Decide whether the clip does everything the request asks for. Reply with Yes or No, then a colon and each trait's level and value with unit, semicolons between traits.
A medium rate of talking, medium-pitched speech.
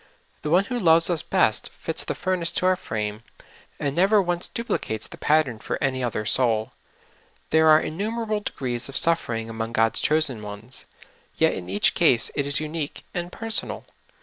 Yes: average, 175 wpm; medium, 150 Hz